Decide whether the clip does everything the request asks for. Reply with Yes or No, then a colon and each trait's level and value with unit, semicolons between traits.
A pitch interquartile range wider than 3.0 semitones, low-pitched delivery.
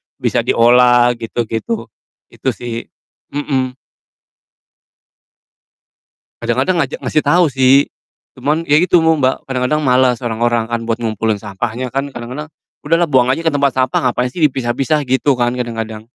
Yes: average, 3.5 semitones; low, 130 Hz